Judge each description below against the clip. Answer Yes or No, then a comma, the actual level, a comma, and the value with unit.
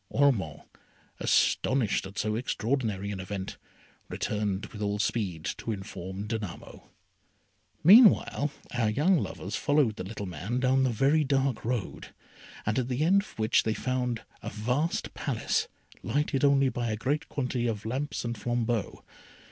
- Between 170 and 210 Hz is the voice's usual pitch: No, low, 120 Hz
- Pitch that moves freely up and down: No, average, 4.5 semitones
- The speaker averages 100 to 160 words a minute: Yes, average, 145 wpm